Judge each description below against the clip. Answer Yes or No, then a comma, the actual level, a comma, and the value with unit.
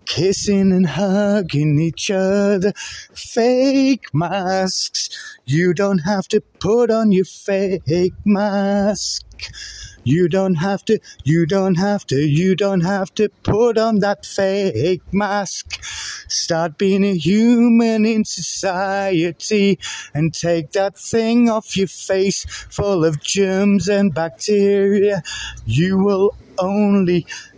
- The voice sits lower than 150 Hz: No, high, 195 Hz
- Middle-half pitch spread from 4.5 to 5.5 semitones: No, narrow, 2.4 semitones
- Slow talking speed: Yes, slow, 120 wpm